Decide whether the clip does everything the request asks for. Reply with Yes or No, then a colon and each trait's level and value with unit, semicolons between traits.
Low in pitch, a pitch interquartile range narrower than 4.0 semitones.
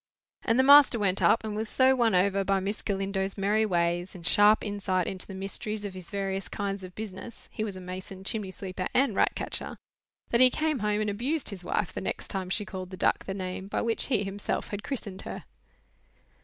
No: high, 200 Hz; narrow, 2.5 semitones